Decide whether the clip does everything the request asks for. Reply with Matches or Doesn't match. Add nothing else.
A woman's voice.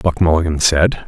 Doesn't match